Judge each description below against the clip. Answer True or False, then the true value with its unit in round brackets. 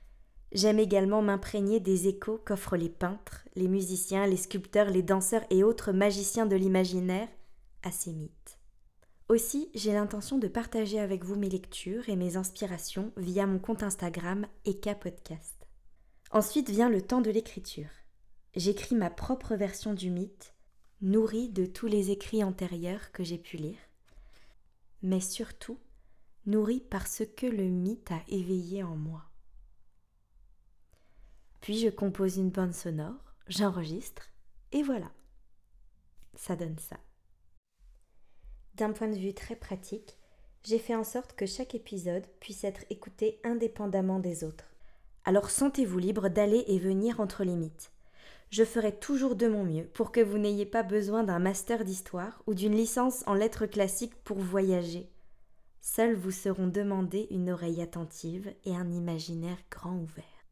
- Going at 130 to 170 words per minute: True (145 wpm)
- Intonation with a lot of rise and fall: False (3.7 semitones)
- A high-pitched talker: True (195 Hz)